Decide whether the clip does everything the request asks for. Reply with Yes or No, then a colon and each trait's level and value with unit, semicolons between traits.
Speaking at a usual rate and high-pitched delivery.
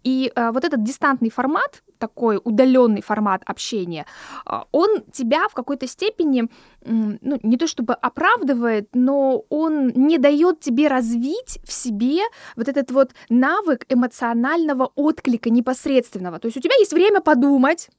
Yes: average, 135 wpm; very high, 260 Hz